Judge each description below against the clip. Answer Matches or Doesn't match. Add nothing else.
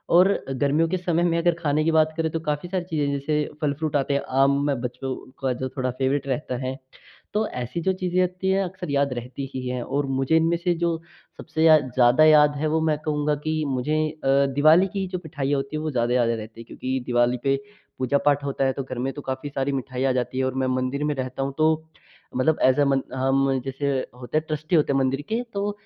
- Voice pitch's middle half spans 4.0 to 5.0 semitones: Doesn't match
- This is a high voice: Doesn't match